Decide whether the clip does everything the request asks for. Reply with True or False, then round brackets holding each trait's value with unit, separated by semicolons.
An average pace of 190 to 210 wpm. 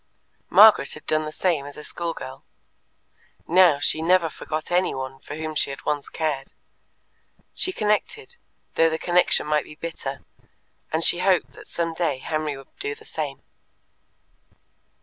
False (150 wpm)